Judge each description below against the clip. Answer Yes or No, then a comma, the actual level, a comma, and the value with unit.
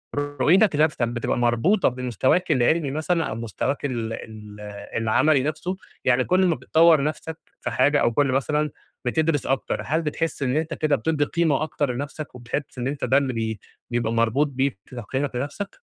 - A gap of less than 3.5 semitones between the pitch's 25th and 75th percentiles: No, average, 4.2 semitones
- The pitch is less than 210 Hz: Yes, medium, 140 Hz